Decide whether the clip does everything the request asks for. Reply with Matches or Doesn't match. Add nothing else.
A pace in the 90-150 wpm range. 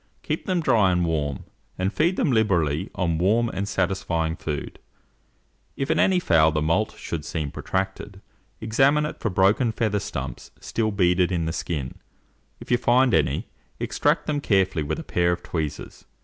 Doesn't match